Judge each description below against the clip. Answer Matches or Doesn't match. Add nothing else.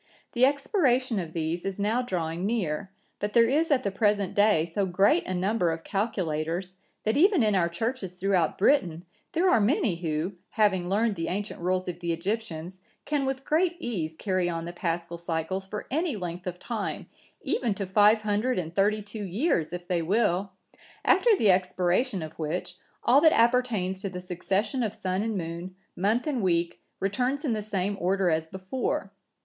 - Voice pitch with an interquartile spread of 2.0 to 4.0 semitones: Doesn't match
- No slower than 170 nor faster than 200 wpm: Matches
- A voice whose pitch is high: Matches